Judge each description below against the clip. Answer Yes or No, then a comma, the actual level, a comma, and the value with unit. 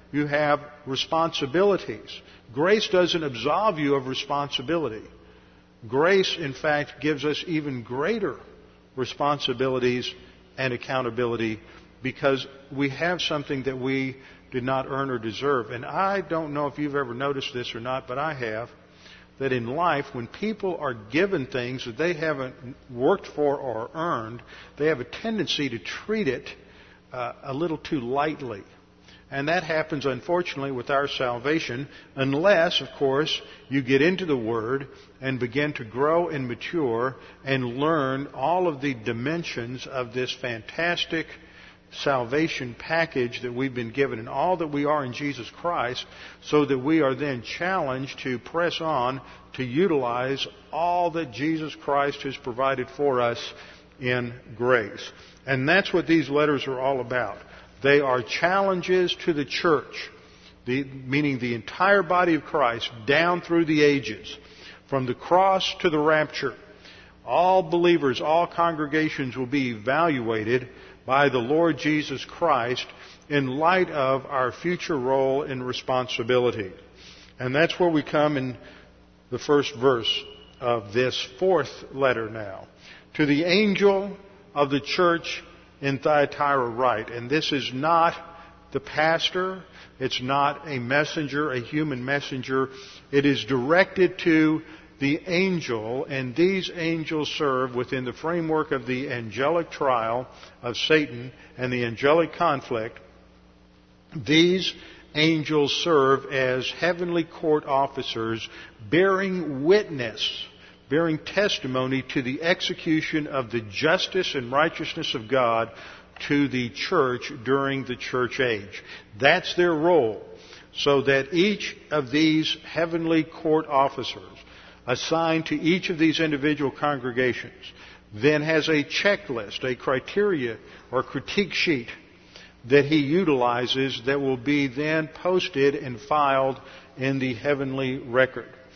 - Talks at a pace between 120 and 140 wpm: Yes, slow, 135 wpm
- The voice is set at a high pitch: No, medium, 140 Hz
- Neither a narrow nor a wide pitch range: Yes, average, 4.0 semitones